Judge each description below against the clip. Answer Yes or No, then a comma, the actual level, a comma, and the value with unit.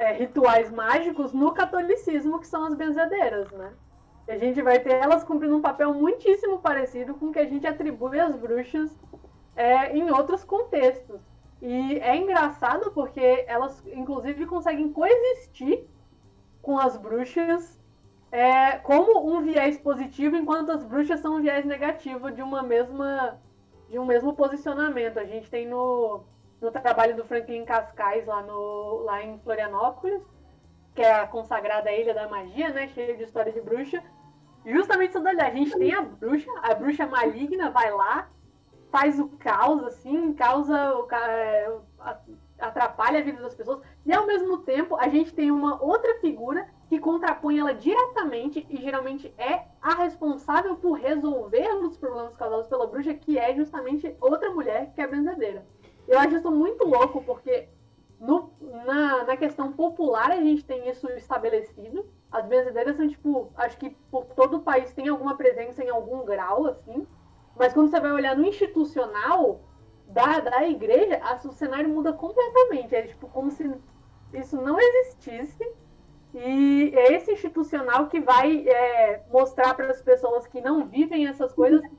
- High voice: Yes, very high, 280 Hz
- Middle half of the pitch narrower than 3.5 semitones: No, average, 4.5 semitones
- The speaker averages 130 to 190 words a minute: Yes, average, 160 wpm